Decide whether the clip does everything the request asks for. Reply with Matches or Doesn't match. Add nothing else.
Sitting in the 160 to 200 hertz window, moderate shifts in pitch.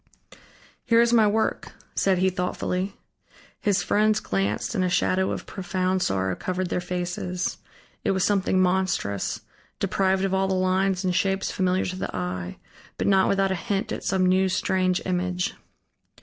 Doesn't match